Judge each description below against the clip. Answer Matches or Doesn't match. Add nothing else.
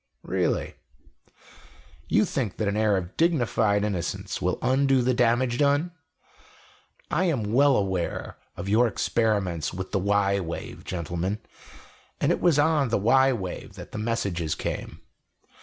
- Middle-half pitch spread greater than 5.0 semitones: Matches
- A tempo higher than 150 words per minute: Doesn't match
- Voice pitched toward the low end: Matches